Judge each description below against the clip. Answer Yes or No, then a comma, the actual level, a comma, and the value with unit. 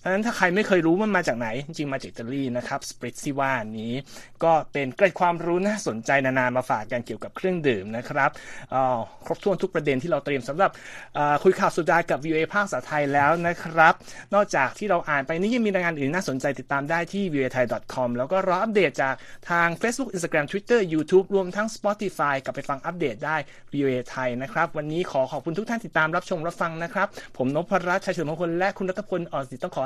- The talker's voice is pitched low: No, medium, 165 Hz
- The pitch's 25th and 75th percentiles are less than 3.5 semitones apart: No, average, 5.3 semitones